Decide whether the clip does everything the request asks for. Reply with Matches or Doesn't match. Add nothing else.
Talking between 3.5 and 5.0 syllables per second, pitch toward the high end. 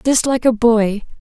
Matches